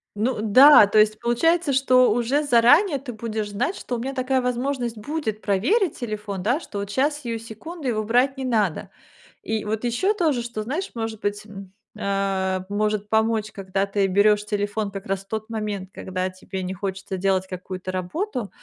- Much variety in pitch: No, average, 4.1 semitones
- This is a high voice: Yes, high, 220 Hz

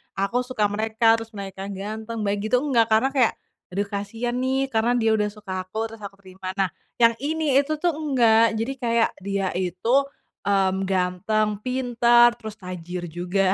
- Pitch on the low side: No, high, 220 Hz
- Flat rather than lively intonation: No, average, 3.6 semitones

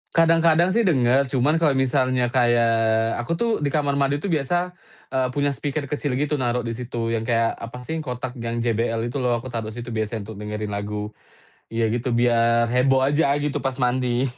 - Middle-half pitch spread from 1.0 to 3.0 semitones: No, average, 3.5 semitones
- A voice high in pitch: No, low, 125 Hz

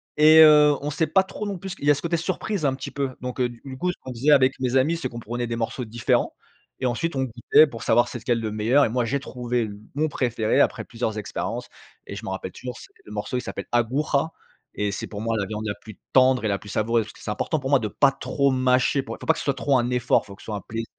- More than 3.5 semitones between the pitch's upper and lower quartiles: Yes, average, 4.0 semitones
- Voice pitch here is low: Yes, low, 125 Hz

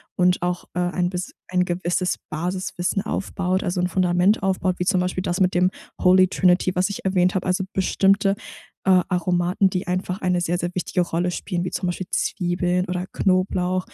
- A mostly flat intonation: Yes, narrow, 0.8 semitones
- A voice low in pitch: No, medium, 180 Hz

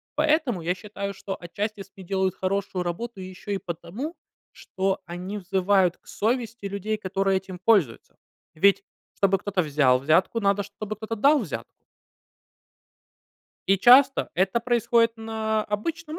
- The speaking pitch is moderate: No, high, 200 Hz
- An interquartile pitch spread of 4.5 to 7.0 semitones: No, average, 3.2 semitones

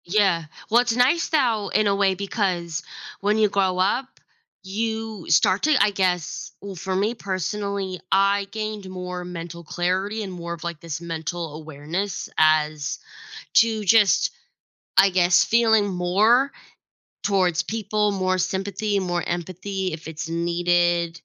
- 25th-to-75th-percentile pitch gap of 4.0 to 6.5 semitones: No, average, 3.2 semitones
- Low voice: No, high, 190 Hz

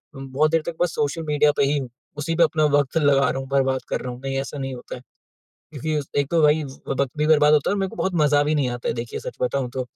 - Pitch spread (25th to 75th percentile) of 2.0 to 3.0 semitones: Yes, narrow, 2.4 semitones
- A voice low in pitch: No, medium, 145 Hz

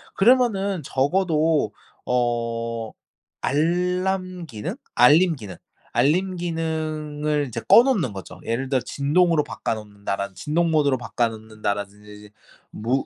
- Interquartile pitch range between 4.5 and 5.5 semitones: No, wide, 7.1 semitones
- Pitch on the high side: No, medium, 145 Hz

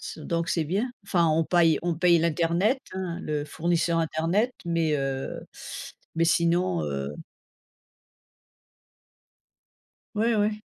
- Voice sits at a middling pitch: Yes, medium, 170 Hz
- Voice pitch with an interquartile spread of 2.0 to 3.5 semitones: Yes, narrow, 2.4 semitones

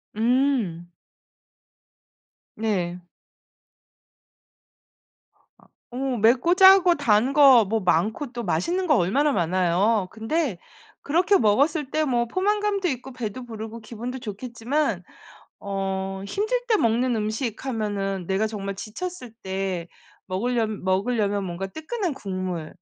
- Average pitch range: No, wide, 6.2 semitones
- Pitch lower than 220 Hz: No, high, 225 Hz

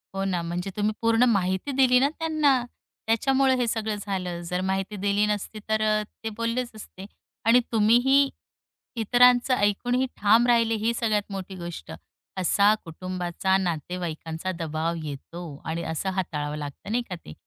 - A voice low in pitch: No, high, 205 Hz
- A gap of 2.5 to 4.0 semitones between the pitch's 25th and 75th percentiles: No, average, 4.6 semitones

